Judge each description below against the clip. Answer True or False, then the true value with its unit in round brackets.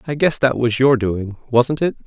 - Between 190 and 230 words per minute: True (205 wpm)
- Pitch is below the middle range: True (125 Hz)